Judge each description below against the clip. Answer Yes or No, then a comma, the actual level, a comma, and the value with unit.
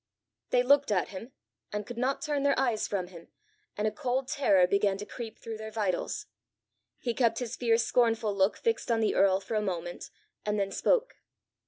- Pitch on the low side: No, high, 220 Hz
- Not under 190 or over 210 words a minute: Yes, average, 195 wpm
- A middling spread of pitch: Yes, average, 3.9 semitones